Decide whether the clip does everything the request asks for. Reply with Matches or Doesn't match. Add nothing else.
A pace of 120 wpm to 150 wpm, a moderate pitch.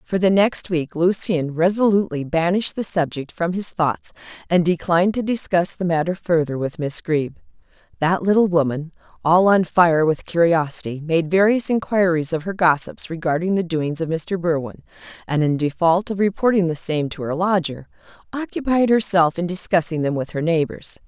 Doesn't match